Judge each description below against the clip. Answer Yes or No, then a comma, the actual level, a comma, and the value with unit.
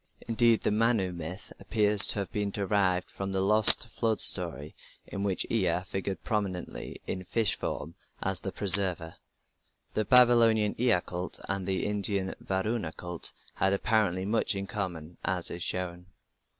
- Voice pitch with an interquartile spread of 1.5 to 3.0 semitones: Yes, average, 2.7 semitones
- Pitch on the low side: Yes, very low, 95 Hz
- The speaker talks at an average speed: Yes, average, 150 wpm